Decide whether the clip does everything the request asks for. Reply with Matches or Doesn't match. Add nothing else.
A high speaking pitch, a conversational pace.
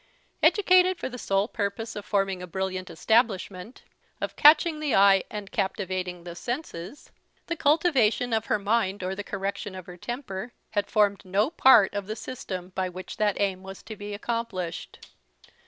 Matches